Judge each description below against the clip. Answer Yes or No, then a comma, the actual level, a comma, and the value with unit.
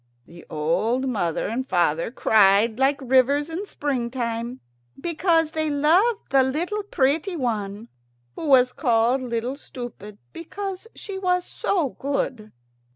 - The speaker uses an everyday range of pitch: No, wide, 5.7 semitones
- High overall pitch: Yes, very high, 260 Hz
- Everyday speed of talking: No, slow, 125 wpm